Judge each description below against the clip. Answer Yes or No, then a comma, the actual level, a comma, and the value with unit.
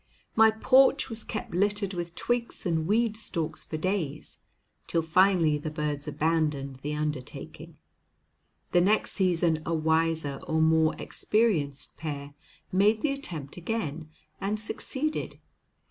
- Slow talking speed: Yes, slow, 130 wpm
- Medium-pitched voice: Yes, medium, 165 Hz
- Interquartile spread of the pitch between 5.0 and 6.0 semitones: Yes, average, 5.3 semitones